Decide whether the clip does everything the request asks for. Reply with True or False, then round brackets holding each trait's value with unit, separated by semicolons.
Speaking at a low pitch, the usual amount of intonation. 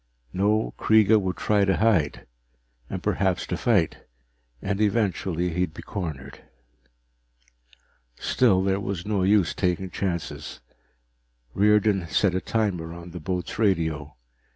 True (95 Hz; 3.2 semitones)